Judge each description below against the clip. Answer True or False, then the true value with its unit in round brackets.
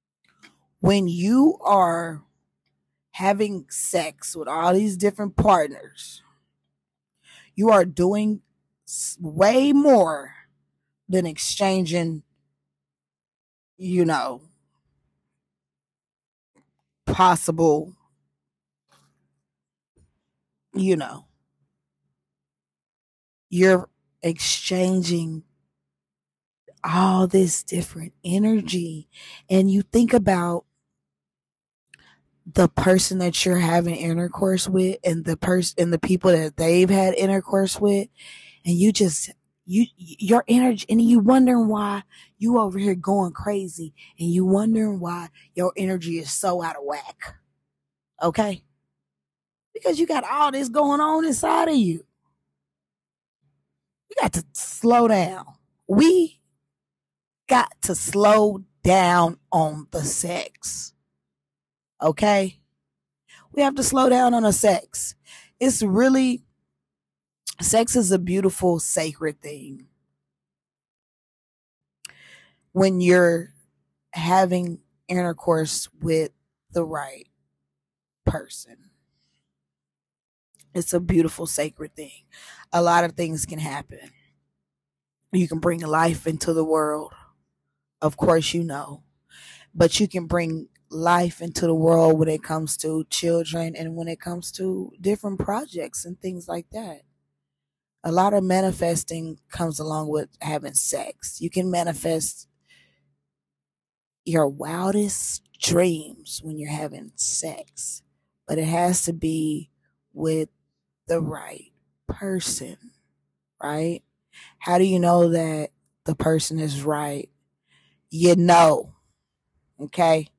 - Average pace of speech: False (105 wpm)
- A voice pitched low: False (165 Hz)